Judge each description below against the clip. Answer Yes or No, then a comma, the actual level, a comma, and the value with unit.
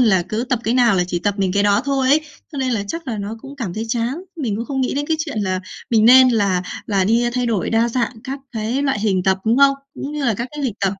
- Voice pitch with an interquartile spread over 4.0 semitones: Yes, average, 4.7 semitones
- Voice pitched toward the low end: No, high, 235 Hz